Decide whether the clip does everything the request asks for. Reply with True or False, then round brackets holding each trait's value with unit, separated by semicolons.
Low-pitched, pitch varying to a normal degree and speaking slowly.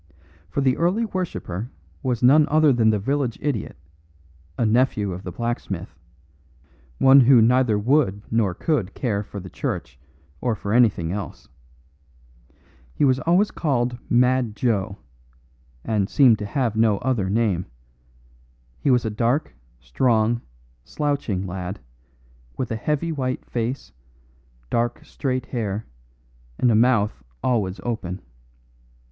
True (115 Hz; 4.2 semitones; 130 wpm)